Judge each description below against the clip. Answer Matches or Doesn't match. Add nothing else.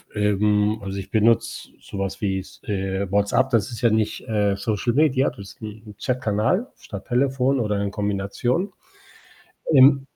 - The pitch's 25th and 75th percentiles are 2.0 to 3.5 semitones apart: Doesn't match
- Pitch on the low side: Matches